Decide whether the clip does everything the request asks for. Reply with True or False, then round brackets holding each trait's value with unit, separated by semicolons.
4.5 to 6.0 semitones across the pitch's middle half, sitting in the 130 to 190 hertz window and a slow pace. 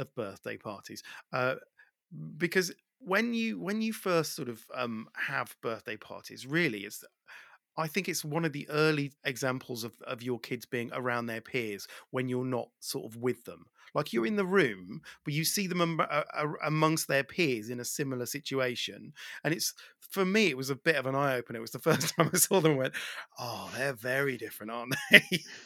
False (5.2 semitones; 140 Hz; 200 wpm)